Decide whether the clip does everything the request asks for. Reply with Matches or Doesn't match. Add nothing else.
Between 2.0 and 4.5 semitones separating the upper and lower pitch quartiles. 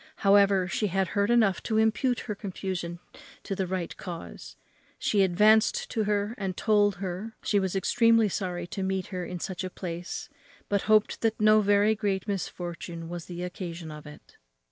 Matches